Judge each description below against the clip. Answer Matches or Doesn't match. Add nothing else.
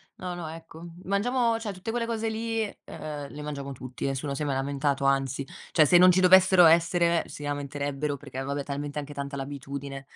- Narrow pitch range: Doesn't match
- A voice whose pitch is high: Doesn't match